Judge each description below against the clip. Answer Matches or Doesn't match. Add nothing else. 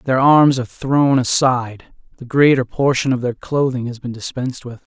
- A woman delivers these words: Doesn't match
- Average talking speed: Matches